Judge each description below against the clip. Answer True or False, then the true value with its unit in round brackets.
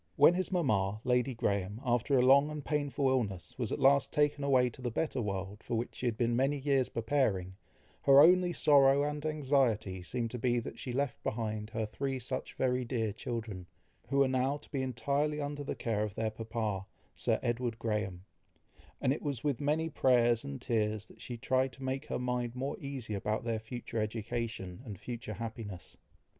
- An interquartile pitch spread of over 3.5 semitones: True (3.9 semitones)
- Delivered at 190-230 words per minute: True (195 wpm)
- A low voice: True (125 Hz)